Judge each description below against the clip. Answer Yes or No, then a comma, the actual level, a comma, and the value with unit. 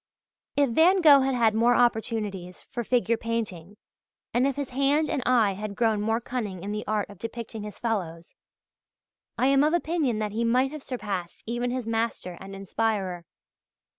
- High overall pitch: Yes, high, 230 Hz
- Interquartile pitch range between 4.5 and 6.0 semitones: No, average, 3.6 semitones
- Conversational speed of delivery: Yes, average, 175 wpm